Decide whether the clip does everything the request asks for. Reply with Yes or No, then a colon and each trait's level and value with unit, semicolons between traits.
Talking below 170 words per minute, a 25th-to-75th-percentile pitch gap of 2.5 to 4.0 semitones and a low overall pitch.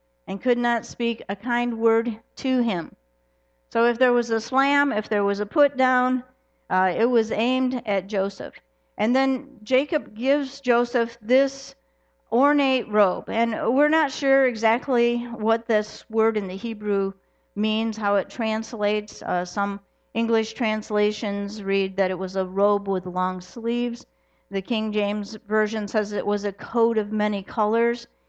No: average, 160 wpm; average, 3.0 semitones; high, 225 Hz